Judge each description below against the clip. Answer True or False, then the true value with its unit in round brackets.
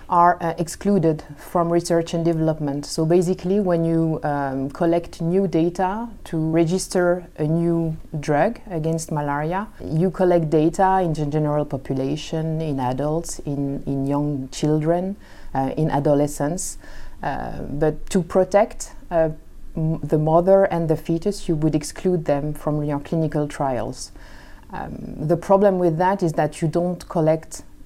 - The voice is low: False (160 Hz)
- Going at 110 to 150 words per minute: True (140 wpm)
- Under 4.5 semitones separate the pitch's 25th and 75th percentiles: True (2.9 semitones)